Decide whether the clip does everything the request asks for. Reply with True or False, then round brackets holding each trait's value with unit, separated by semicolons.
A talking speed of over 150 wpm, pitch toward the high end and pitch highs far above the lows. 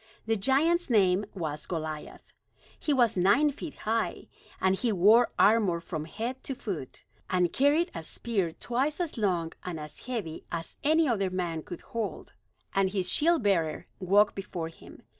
True (160 wpm; 200 Hz; 6.1 semitones)